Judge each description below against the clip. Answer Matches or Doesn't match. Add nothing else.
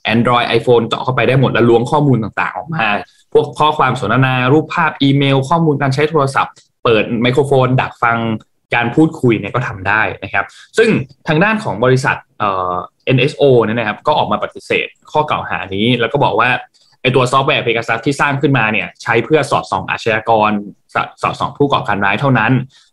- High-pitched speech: Doesn't match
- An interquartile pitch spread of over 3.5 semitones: Matches